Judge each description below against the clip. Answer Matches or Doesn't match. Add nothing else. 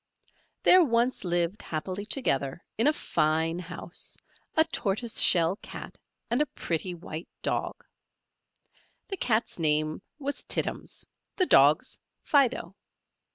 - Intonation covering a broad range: Matches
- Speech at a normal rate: Doesn't match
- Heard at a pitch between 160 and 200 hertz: Matches